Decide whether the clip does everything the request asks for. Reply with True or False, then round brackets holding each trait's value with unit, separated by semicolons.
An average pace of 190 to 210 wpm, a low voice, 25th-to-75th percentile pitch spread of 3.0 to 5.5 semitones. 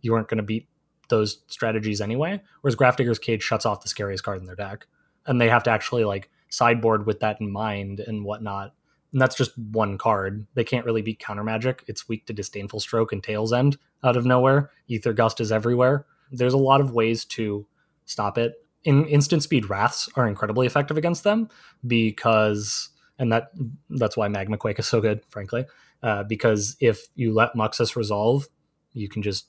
True (195 wpm; 115 Hz; 3.3 semitones)